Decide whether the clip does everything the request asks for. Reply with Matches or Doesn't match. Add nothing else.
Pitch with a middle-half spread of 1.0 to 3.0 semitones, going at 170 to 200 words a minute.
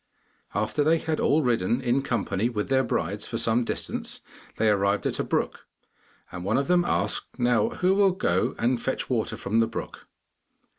Doesn't match